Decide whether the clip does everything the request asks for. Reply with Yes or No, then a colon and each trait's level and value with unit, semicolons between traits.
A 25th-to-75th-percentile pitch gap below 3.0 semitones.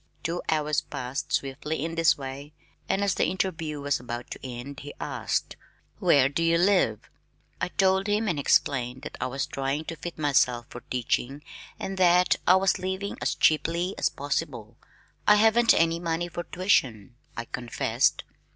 No: average, 5.2 semitones